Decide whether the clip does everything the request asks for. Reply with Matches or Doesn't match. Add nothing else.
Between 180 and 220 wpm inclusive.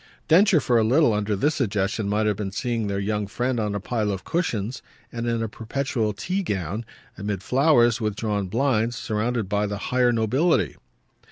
Matches